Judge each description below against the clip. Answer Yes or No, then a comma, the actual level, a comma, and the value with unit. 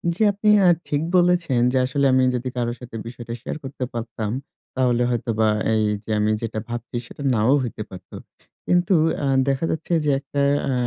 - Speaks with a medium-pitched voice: No, low, 125 Hz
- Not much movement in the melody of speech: No, average, 3.5 semitones